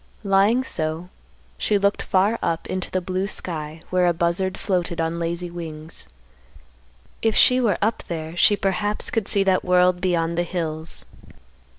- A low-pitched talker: No, medium, 180 Hz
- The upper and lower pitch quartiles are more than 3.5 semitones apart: No, average, 2.8 semitones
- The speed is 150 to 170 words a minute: Yes, average, 160 wpm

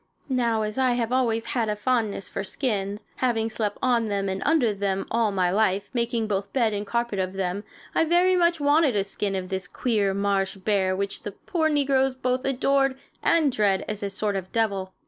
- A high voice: Yes, high, 215 Hz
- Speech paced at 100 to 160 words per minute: No, fast, 205 wpm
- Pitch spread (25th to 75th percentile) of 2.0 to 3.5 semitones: No, average, 4.4 semitones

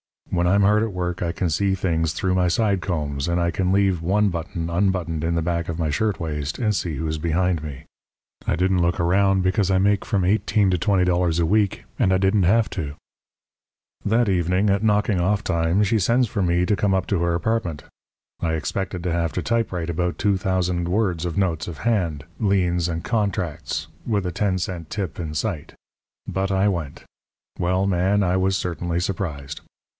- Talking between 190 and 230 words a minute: Yes, average, 200 wpm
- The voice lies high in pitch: No, very low, 90 Hz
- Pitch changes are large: No, average, 2.8 semitones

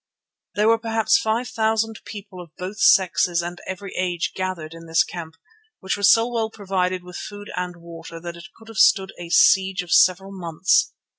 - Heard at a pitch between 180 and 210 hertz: Yes, high, 190 Hz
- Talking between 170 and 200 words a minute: Yes, average, 190 wpm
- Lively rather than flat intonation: No, average, 3.7 semitones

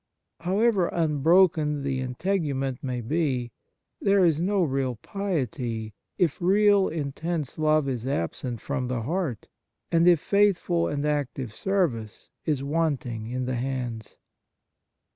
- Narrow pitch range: No, average, 5.3 semitones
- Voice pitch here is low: No, medium, 145 Hz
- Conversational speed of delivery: No, slow, 125 wpm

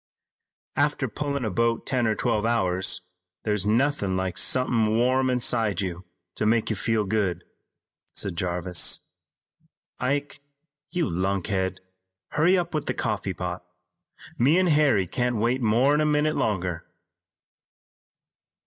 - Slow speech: Yes, slow, 130 wpm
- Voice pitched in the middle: No, low, 115 Hz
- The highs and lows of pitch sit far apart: Yes, wide, 6.0 semitones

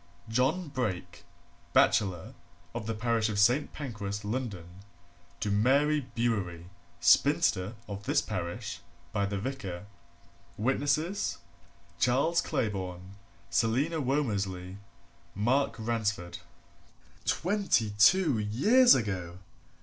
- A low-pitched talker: Yes, low, 110 Hz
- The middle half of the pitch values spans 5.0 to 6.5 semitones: Yes, wide, 5.5 semitones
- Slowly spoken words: Yes, slow, 95 wpm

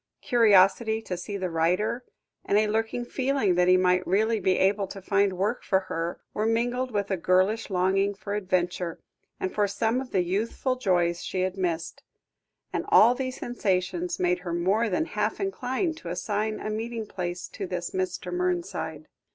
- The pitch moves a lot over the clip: No, average, 3.7 semitones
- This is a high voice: Yes, high, 200 Hz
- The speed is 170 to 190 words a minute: Yes, average, 175 wpm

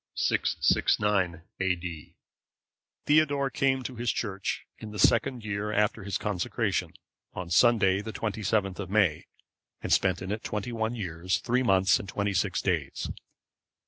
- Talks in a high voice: No, low, 105 Hz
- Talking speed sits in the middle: Yes, average, 145 wpm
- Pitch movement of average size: Yes, average, 3.4 semitones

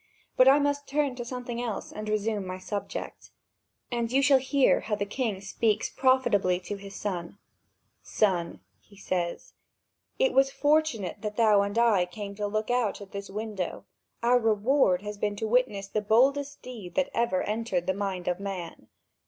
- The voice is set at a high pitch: Yes, high, 215 Hz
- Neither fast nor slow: Yes, average, 170 wpm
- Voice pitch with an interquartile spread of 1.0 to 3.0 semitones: No, average, 4.0 semitones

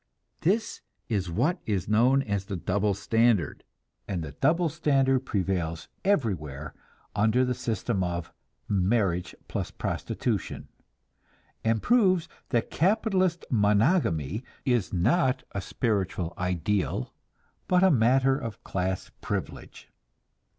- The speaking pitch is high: No, low, 110 Hz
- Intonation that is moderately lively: No, wide, 6.3 semitones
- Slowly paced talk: Yes, slow, 110 wpm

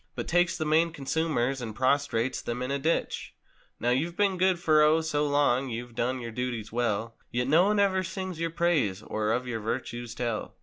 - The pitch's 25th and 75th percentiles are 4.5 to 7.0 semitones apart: Yes, wide, 5.5 semitones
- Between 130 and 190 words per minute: No, average, 200 wpm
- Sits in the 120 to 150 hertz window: Yes, low, 135 Hz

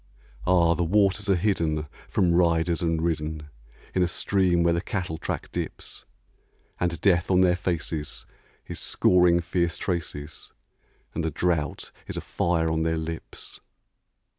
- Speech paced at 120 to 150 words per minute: Yes, average, 145 wpm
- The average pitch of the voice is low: Yes, very low, 85 Hz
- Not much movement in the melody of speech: Yes, narrow, 1.8 semitones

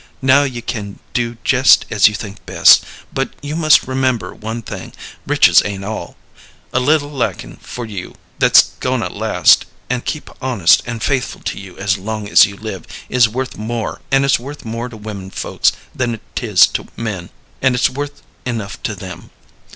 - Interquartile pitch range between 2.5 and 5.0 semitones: Yes, average, 3.9 semitones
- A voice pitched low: Yes, low, 115 Hz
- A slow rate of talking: No, average, 180 wpm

